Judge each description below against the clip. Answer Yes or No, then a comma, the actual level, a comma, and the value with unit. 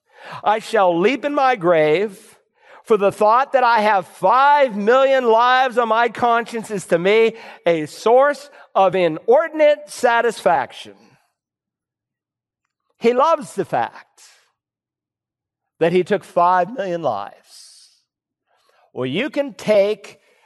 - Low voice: No, high, 225 Hz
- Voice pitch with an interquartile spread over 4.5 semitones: Yes, average, 5.2 semitones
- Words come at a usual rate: No, slow, 115 wpm